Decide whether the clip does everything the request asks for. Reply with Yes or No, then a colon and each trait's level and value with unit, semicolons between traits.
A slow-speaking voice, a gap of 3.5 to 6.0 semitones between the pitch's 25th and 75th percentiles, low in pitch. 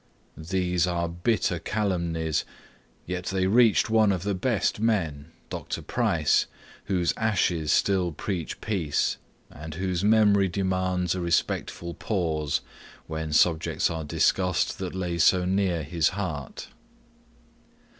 No: slow, 125 wpm; average, 2.8 semitones; very low, 90 Hz